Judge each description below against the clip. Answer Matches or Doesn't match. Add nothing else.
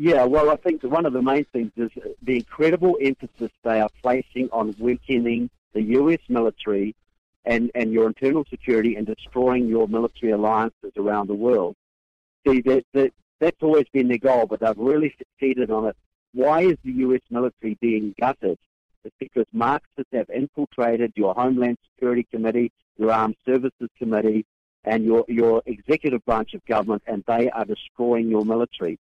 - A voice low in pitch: Matches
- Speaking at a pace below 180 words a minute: Matches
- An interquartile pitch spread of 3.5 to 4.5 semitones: Doesn't match